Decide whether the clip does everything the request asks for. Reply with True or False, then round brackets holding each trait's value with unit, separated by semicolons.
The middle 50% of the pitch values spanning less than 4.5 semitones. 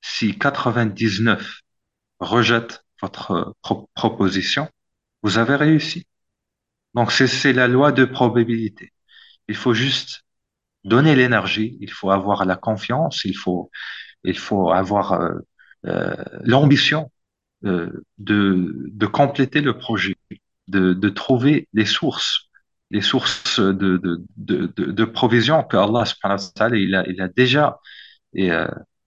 False (4.9 semitones)